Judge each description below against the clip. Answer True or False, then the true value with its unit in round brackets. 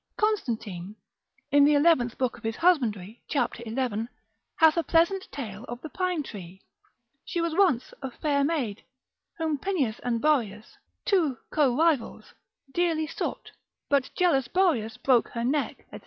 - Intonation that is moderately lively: False (6.0 semitones)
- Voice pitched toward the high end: True (275 Hz)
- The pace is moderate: True (150 wpm)